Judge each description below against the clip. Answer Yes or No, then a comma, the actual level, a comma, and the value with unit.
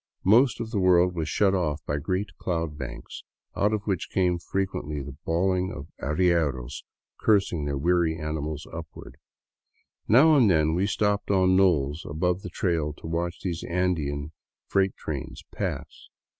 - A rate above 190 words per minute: No, average, 155 wpm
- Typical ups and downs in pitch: Yes, average, 3.8 semitones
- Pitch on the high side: No, very low, 85 Hz